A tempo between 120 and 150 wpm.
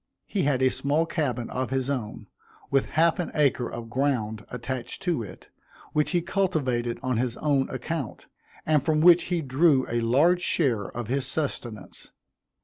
No: average, 165 wpm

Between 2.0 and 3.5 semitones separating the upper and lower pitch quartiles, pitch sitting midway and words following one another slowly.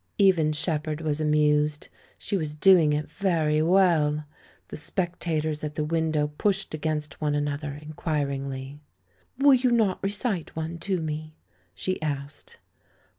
Yes: average, 2.7 semitones; medium, 155 Hz; slow, 130 wpm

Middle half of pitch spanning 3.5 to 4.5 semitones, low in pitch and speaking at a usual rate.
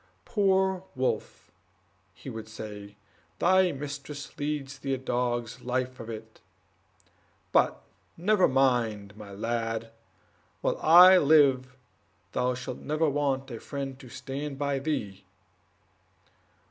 No: average, 4.0 semitones; low, 130 Hz; slow, 115 wpm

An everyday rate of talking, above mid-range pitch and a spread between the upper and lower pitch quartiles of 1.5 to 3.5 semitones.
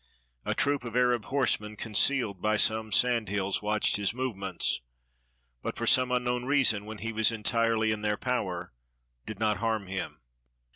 No: average, 160 wpm; low, 110 Hz; average, 2.9 semitones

